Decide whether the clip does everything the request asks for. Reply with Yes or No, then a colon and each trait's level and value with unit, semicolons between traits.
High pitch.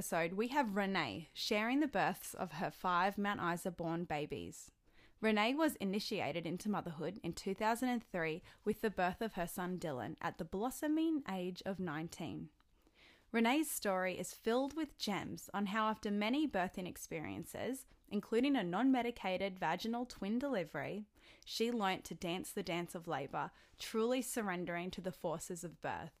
Yes: high, 195 Hz